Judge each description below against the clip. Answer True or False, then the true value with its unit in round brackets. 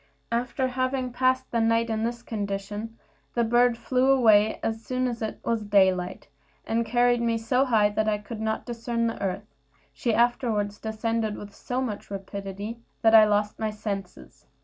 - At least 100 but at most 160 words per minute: False (170 wpm)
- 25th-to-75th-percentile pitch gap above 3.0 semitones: False (2.5 semitones)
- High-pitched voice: True (225 Hz)